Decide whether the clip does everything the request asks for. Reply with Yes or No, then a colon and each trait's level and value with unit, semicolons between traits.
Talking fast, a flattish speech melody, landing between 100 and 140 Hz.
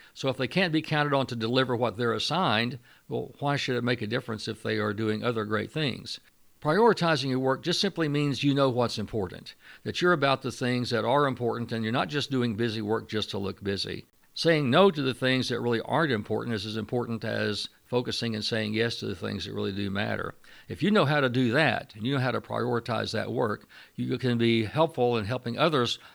No: fast, 230 wpm; average, 3.7 semitones; low, 120 Hz